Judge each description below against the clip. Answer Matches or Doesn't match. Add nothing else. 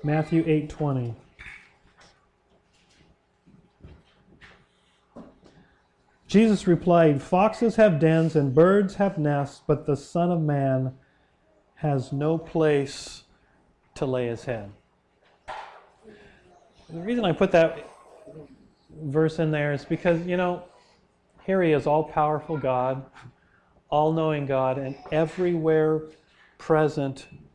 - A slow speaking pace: Matches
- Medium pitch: Matches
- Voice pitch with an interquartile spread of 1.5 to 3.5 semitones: Matches